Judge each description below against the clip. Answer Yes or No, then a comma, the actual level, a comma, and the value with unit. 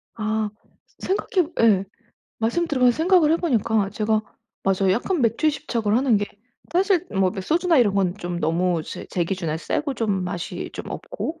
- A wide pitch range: Yes, wide, 8.2 semitones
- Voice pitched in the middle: No, high, 220 Hz